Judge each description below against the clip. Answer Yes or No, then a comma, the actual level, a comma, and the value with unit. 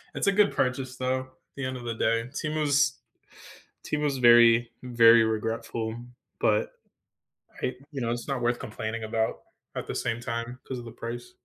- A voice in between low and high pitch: No, low, 120 Hz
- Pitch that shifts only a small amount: Yes, narrow, 2.1 semitones